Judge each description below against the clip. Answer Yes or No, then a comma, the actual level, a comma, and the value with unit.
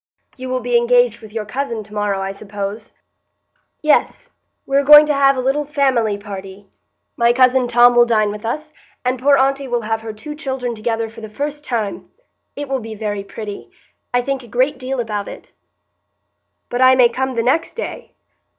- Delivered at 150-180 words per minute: No, average, 195 wpm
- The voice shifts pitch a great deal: No, average, 3.7 semitones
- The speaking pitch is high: Yes, high, 245 Hz